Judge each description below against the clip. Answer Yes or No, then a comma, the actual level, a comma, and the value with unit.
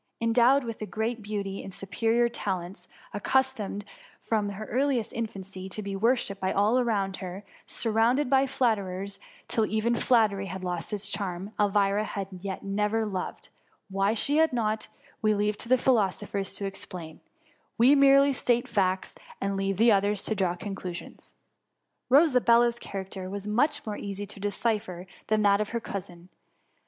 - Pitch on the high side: Yes, high, 210 Hz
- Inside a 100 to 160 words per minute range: Yes, average, 150 wpm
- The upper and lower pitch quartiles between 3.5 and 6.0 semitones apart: No, average, 3.1 semitones